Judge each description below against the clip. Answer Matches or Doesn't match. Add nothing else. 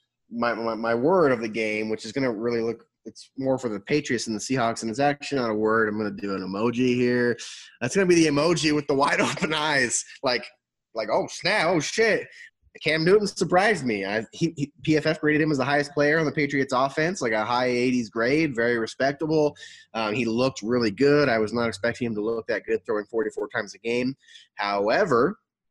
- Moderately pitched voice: Doesn't match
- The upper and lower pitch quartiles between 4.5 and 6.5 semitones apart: Matches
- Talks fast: Matches